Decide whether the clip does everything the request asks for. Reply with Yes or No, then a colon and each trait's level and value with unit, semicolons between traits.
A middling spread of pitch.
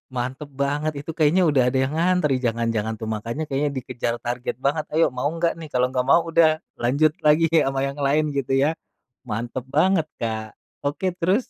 Yes: average, 4.1 semitones